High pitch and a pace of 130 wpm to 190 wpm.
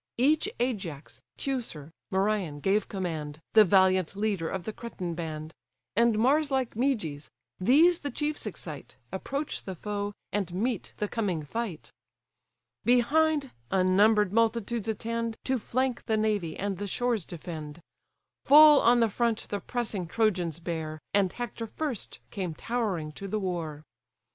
Yes: high, 210 Hz; average, 140 wpm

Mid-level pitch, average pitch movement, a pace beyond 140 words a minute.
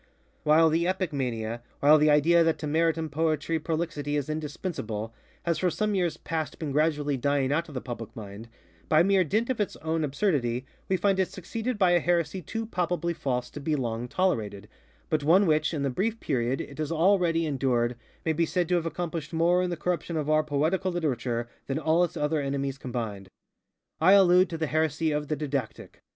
Yes: medium, 155 Hz; average, 3.8 semitones; average, 200 wpm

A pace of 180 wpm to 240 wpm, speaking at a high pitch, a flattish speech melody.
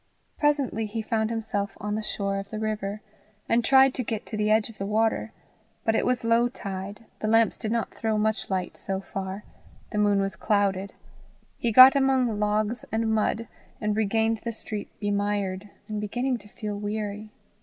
Yes: average, 185 wpm; high, 215 Hz; narrow, 1.8 semitones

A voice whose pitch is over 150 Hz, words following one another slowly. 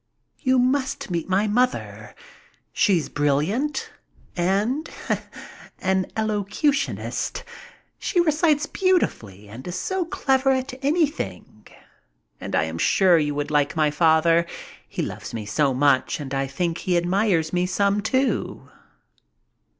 Yes: medium, 185 Hz; slow, 125 wpm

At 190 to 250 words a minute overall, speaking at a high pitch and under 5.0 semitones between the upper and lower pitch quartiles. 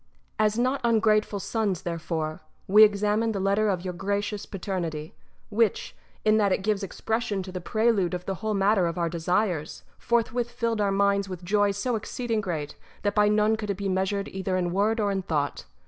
Yes: average, 200 wpm; high, 200 Hz; narrow, 2.6 semitones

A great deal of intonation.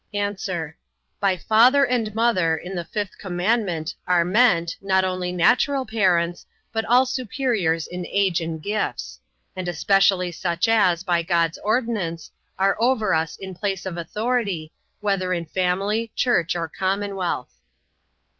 No: average, 3.9 semitones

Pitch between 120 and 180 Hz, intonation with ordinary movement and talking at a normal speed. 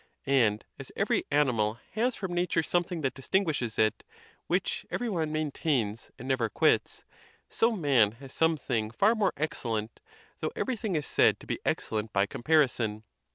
No: medium, 140 Hz; wide, 7.5 semitones; average, 160 wpm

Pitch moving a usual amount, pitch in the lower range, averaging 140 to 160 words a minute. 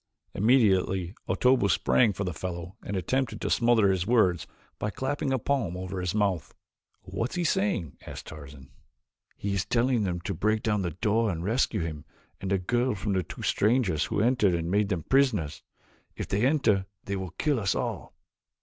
No: average, 4.7 semitones; low, 100 Hz; average, 185 wpm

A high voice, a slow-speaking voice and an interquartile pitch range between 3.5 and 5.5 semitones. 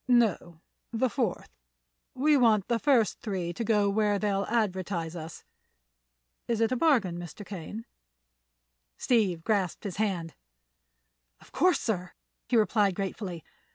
Yes: high, 205 Hz; slow, 130 wpm; average, 4.2 semitones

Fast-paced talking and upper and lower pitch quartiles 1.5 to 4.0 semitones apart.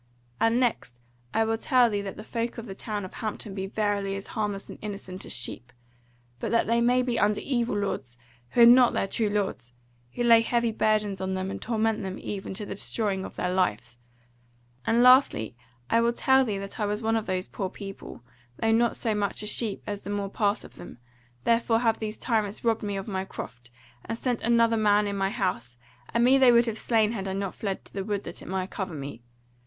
Yes: fast, 225 wpm; average, 2.9 semitones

